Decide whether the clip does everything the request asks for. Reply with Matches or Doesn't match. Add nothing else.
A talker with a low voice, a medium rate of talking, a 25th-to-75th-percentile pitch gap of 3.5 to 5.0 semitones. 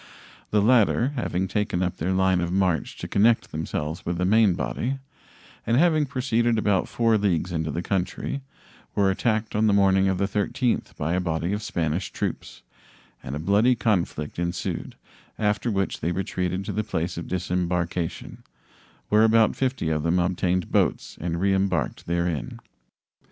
Matches